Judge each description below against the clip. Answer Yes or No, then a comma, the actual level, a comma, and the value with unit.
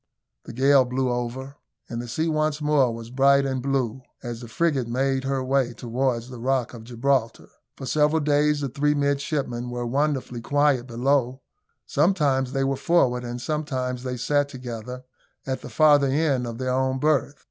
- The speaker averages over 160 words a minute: Yes, average, 175 wpm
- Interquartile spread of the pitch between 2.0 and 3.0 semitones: Yes, narrow, 2.6 semitones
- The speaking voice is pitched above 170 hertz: No, low, 130 Hz